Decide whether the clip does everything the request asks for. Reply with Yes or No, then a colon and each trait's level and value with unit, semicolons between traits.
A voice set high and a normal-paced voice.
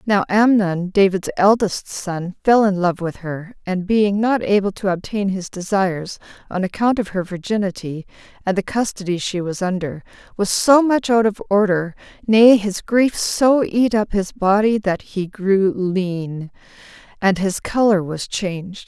Yes: high, 195 Hz; average, 165 wpm